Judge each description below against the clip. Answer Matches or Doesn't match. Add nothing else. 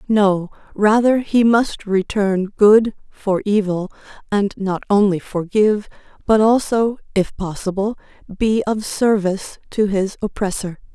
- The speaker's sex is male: Doesn't match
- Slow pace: Matches